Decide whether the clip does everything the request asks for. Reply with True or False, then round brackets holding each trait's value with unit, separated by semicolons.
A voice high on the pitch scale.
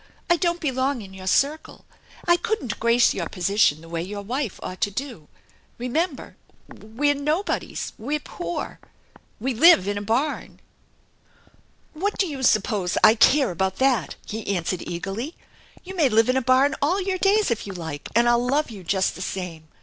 True (240 Hz)